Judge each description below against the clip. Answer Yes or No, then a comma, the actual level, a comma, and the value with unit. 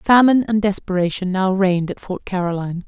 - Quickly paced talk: No, average, 165 wpm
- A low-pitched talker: No, high, 195 Hz